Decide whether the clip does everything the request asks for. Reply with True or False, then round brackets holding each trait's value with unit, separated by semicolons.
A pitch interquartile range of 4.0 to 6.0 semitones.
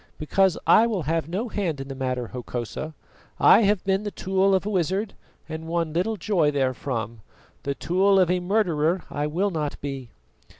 True (5.2 semitones)